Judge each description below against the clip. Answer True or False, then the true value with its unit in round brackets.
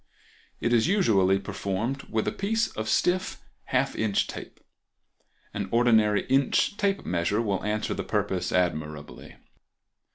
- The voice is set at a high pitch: False (110 Hz)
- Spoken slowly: True (130 wpm)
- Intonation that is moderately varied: False (5.9 semitones)